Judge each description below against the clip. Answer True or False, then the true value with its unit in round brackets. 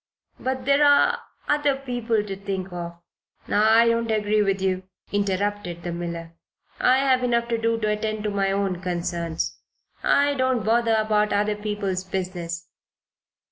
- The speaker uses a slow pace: False (155 wpm)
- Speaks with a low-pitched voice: False (210 Hz)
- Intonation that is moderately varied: True (3.7 semitones)